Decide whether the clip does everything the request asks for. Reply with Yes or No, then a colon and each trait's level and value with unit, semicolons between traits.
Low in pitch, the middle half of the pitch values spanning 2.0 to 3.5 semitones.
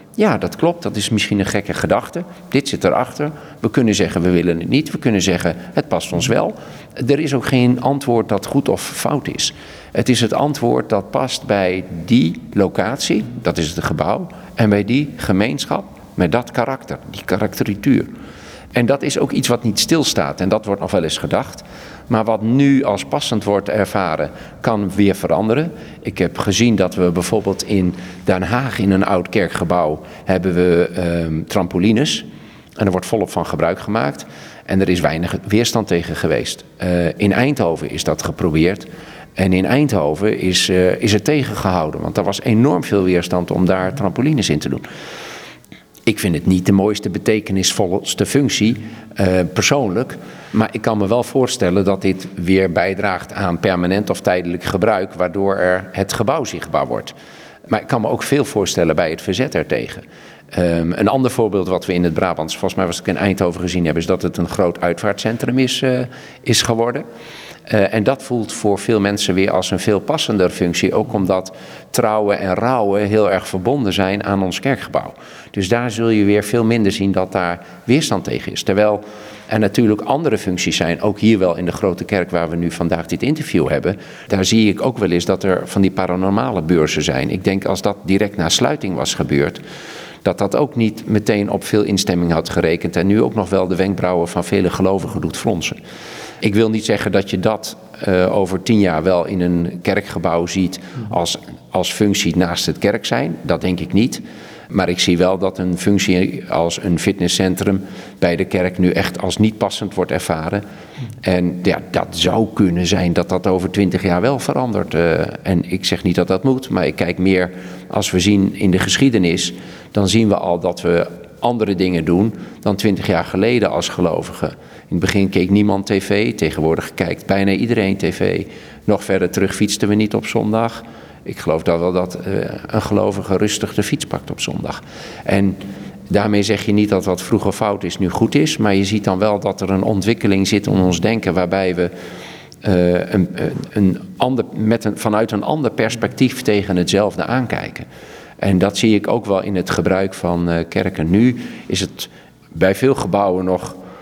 Yes: low, 100 Hz; average, 3.2 semitones